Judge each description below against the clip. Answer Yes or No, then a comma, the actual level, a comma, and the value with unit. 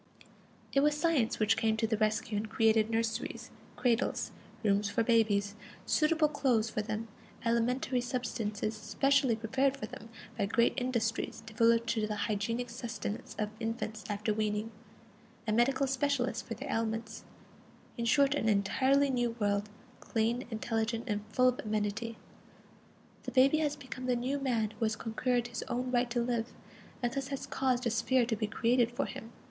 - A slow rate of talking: No, average, 165 wpm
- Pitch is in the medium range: No, high, 230 Hz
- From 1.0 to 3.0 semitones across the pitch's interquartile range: Yes, narrow, 2.6 semitones